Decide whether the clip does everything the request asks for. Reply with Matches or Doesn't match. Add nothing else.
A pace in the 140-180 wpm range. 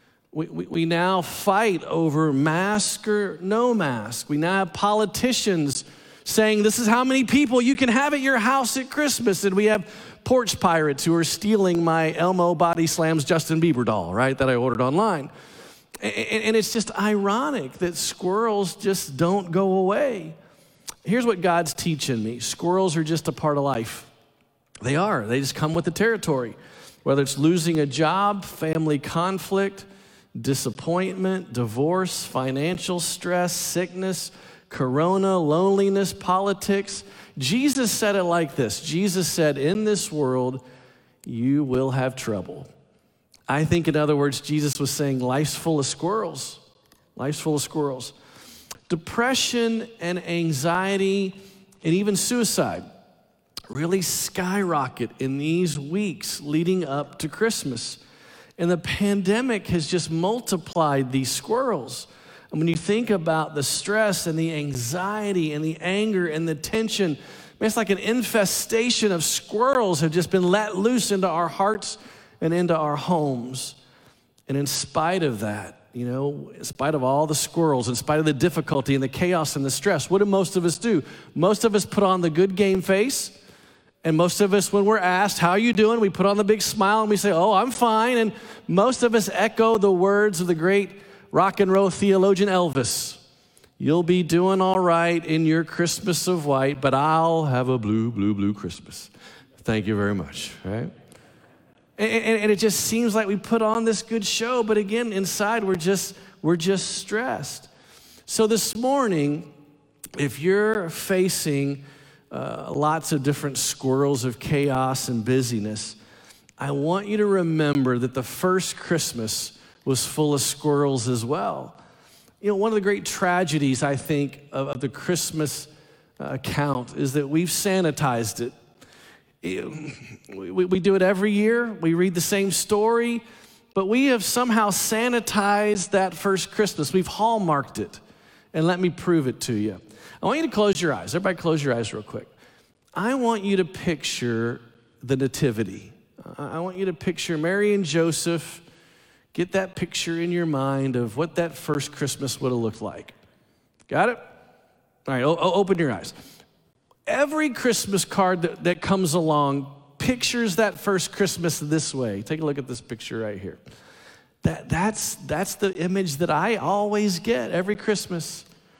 Matches